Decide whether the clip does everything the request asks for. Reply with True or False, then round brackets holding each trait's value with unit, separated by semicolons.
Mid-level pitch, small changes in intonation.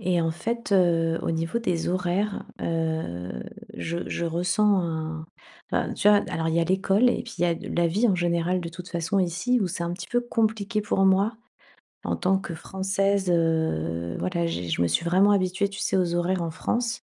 False (175 Hz; 3.0 semitones)